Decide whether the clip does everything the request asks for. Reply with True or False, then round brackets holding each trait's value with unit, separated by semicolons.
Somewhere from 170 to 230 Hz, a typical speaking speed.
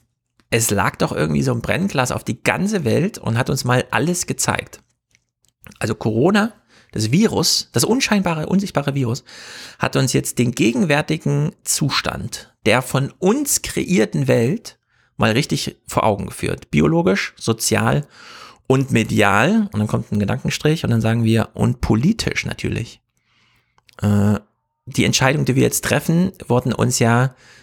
False (125 Hz; 145 wpm)